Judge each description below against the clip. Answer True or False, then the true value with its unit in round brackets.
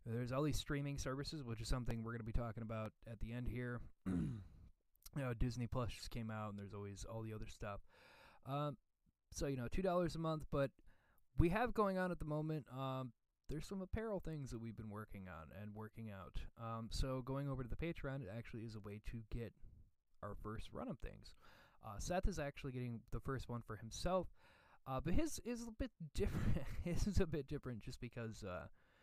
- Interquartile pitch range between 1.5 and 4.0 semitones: False (4.6 semitones)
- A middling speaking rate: False (215 wpm)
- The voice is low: True (120 Hz)